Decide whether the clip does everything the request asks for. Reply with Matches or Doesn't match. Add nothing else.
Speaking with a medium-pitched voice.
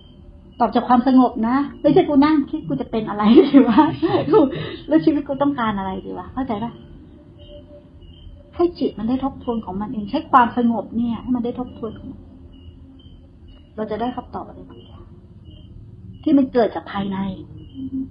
Doesn't match